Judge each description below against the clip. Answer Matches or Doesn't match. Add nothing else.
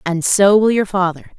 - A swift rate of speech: Matches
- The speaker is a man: Doesn't match